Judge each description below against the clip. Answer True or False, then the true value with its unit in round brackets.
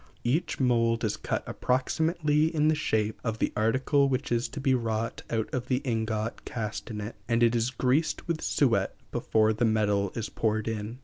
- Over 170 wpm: True (190 wpm)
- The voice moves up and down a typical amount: True (3.3 semitones)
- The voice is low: True (115 Hz)